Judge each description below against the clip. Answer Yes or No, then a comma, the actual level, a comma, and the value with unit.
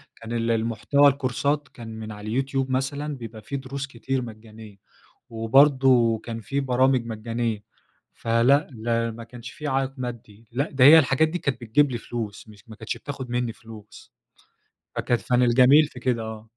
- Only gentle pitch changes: No, average, 3.0 semitones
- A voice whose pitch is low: Yes, low, 120 Hz